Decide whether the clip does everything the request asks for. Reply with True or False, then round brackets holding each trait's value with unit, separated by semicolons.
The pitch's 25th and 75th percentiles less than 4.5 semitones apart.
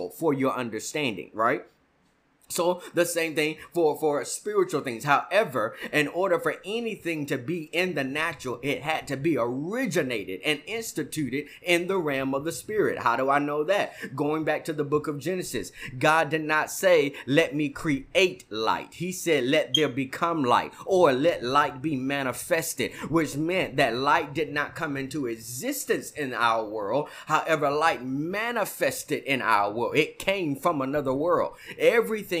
True (3.7 semitones)